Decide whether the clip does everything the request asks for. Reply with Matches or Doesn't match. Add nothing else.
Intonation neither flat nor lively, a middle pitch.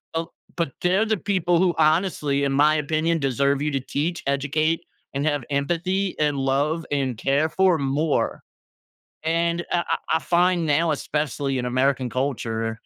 Matches